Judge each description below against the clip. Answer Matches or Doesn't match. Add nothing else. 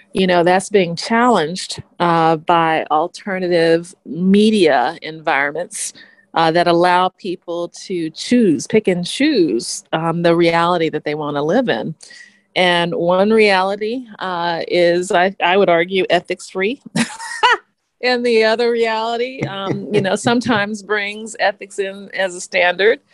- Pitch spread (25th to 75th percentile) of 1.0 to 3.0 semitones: Doesn't match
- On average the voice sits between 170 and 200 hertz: Matches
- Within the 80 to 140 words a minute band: Matches